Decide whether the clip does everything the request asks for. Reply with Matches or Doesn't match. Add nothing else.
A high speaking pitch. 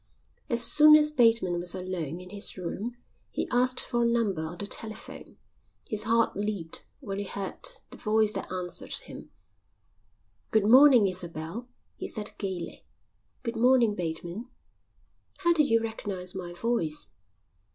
Matches